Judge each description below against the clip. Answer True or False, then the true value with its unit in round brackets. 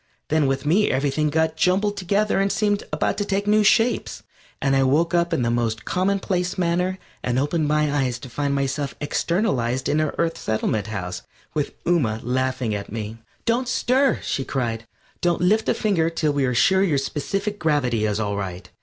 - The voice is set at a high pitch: False (150 Hz)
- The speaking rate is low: False (190 wpm)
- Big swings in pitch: True (6.7 semitones)